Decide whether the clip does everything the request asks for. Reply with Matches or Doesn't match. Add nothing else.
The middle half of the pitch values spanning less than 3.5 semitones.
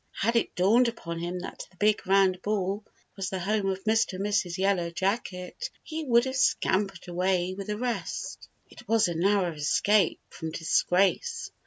Matches